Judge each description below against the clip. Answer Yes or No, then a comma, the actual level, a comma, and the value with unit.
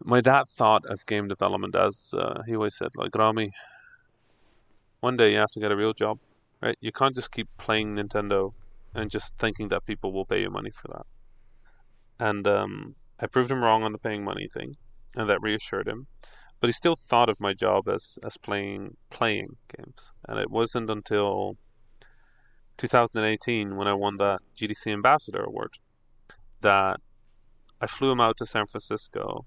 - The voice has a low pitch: Yes, low, 110 Hz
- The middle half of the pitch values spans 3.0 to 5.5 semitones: No, narrow, 2.4 semitones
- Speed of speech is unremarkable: Yes, average, 175 wpm